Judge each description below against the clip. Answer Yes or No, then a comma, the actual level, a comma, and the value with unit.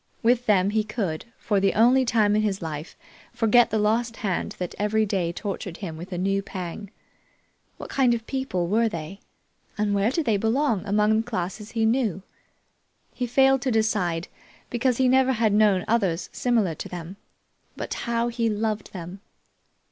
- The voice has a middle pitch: No, high, 215 Hz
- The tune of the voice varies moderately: Yes, average, 3.6 semitones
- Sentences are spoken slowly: No, average, 175 wpm